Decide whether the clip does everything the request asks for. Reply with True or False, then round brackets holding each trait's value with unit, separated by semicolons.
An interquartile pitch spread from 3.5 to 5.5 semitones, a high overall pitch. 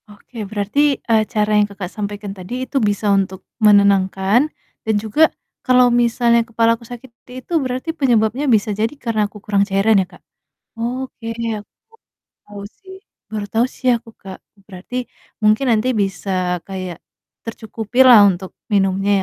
False (3.1 semitones; 215 Hz)